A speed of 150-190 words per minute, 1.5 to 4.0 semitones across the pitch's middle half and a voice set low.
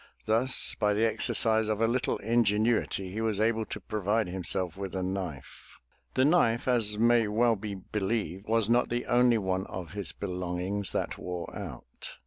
Yes: average, 170 wpm; average, 3.2 semitones; low, 105 Hz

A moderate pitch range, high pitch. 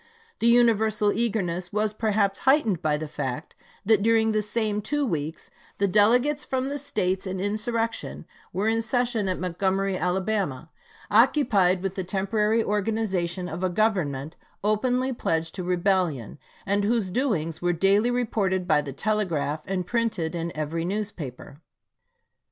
Yes: average, 4.0 semitones; high, 200 Hz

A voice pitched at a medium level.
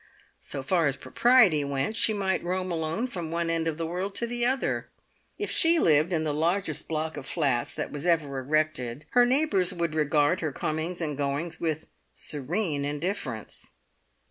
Yes: medium, 160 Hz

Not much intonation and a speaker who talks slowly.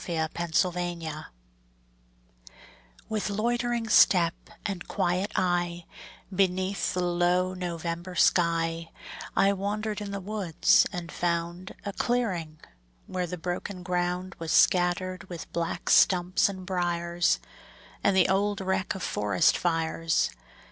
Yes: narrow, 2.0 semitones; slow, 115 wpm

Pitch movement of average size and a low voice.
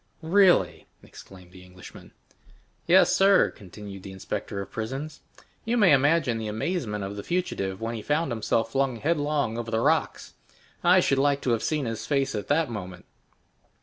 No: wide, 6.4 semitones; low, 120 Hz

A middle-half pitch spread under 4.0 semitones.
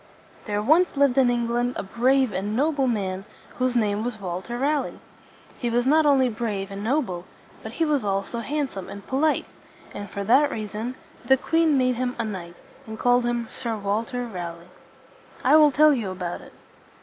No: average, 4.8 semitones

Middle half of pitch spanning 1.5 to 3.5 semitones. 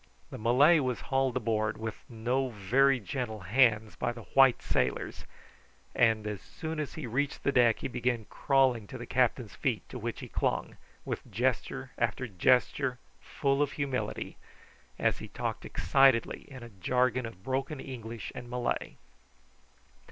Yes: average, 3.0 semitones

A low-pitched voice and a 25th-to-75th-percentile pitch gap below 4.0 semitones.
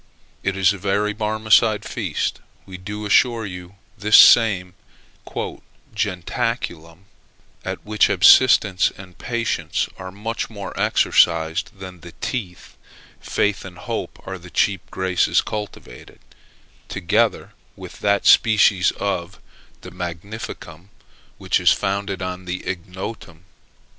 Yes: very low, 95 Hz; average, 2.7 semitones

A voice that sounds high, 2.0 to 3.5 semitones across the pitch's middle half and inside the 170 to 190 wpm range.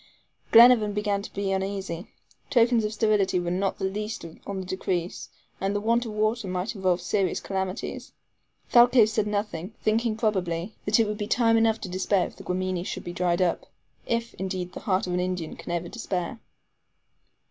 Yes: high, 200 Hz; average, 3.1 semitones; average, 185 wpm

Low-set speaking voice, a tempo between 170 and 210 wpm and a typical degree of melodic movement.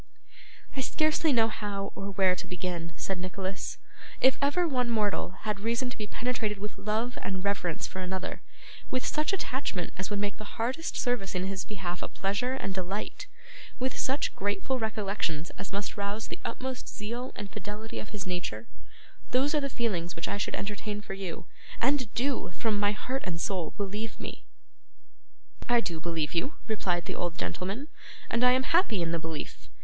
No: high, 205 Hz; average, 180 wpm; average, 4.7 semitones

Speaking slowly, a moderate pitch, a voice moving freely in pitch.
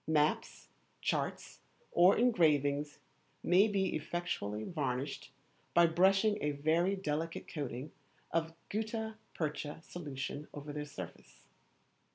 No: slow, 105 wpm; medium, 155 Hz; average, 3.9 semitones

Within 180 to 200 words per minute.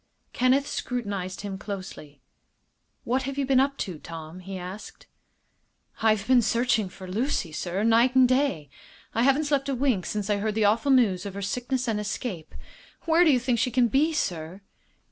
Yes: average, 185 wpm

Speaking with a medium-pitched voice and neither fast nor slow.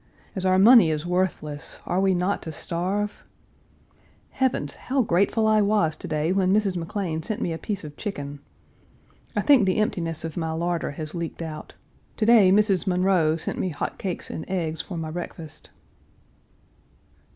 Yes: medium, 180 Hz; average, 170 wpm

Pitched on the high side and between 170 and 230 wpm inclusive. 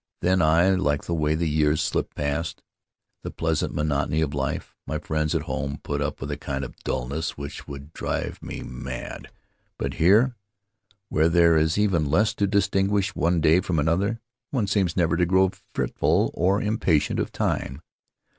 No: very low, 80 Hz; average, 180 wpm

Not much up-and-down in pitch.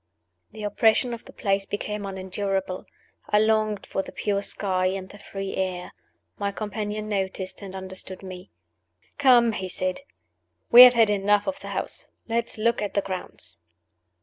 Yes: narrow, 2.2 semitones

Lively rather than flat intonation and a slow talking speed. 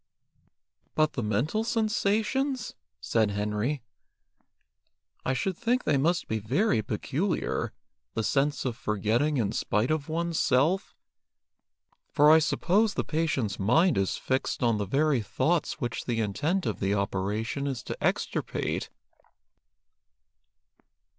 Yes: wide, 7.7 semitones; slow, 125 wpm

